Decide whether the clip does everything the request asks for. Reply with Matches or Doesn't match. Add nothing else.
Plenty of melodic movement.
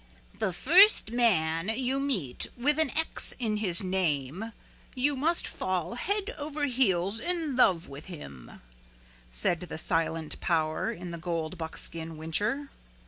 Matches